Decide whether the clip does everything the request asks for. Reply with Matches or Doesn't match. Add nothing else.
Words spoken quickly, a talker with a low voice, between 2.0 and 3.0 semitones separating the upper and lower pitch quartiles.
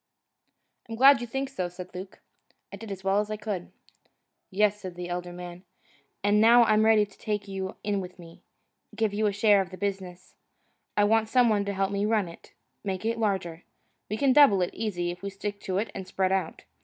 Doesn't match